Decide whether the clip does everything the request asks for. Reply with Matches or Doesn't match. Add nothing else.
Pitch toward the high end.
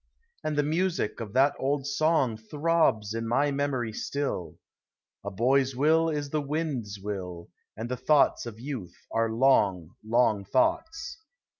Doesn't match